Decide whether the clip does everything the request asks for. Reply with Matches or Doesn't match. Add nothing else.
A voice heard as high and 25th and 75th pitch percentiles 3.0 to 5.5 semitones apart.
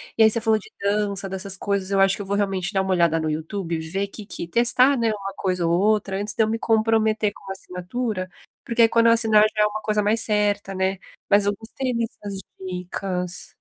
Doesn't match